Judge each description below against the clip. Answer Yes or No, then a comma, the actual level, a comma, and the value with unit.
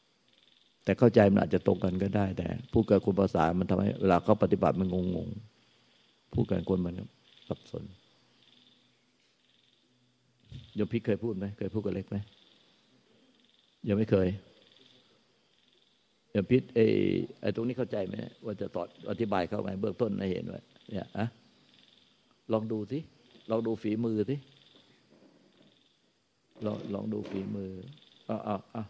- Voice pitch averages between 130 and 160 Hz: No, low, 105 Hz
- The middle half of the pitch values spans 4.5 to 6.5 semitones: No, average, 2.8 semitones